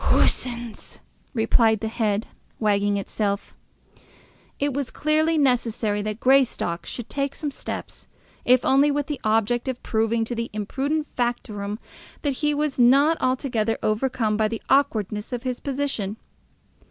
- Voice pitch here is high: Yes, high, 240 Hz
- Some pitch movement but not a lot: Yes, average, 4.2 semitones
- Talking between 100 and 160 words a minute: Yes, average, 140 wpm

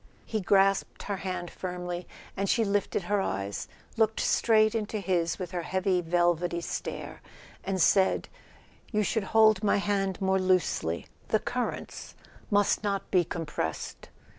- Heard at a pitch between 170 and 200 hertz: Yes, high, 190 Hz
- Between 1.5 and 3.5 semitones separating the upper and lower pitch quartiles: Yes, narrow, 2.6 semitones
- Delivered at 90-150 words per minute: Yes, average, 140 wpm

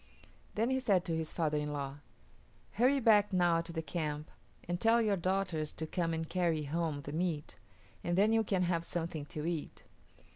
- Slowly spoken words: No, average, 190 wpm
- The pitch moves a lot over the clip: No, average, 3.8 semitones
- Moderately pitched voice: Yes, medium, 170 Hz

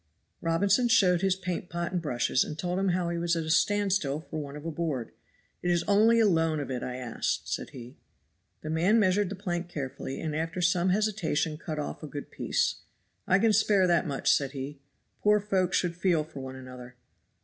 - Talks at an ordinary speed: No, fast, 210 wpm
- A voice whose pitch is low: No, medium, 170 Hz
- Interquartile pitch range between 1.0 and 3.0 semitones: No, average, 4.3 semitones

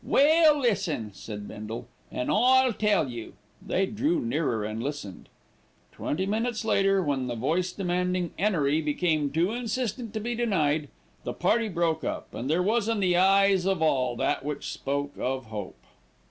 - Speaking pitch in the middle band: Yes, medium, 180 Hz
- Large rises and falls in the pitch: Yes, wide, 7.2 semitones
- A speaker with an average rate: Yes, average, 160 wpm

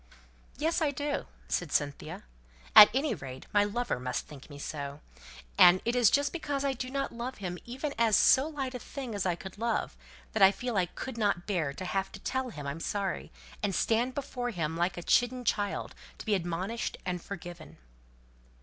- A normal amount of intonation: No, wide, 6.4 semitones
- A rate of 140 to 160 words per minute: No, average, 195 wpm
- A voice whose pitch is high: Yes, high, 205 Hz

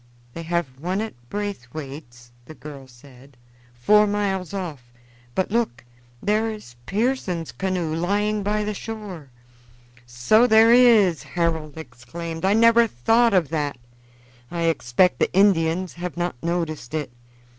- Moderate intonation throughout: No, wide, 5.8 semitones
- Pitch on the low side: No, medium, 175 Hz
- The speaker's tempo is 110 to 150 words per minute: Yes, slow, 135 wpm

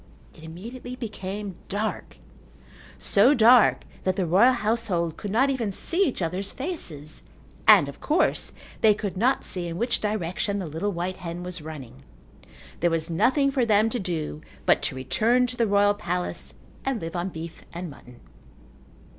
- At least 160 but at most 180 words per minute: Yes, average, 165 wpm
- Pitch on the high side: Yes, high, 195 Hz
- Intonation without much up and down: No, wide, 5.5 semitones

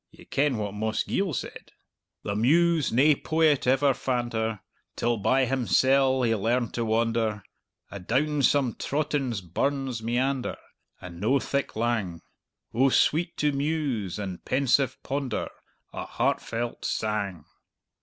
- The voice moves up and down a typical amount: Yes, average, 3.9 semitones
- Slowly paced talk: Yes, slow, 125 wpm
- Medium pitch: No, low, 125 Hz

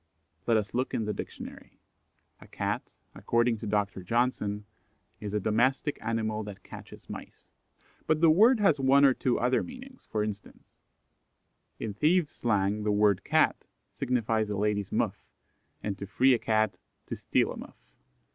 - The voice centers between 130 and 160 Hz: No, low, 110 Hz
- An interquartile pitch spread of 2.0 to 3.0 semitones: No, average, 4.0 semitones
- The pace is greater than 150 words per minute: Yes, average, 160 wpm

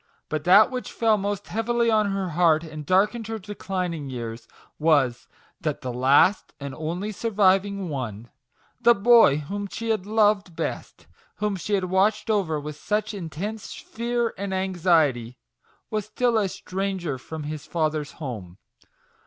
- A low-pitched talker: No, medium, 185 Hz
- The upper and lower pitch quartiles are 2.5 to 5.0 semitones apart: No, wide, 5.6 semitones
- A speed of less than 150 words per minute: No, average, 165 wpm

